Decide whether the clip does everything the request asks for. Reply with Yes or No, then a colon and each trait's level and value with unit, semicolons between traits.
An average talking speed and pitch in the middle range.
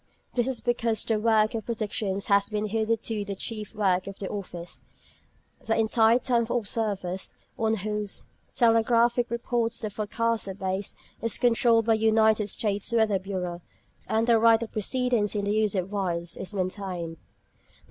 No: average, 170 wpm; high, 215 Hz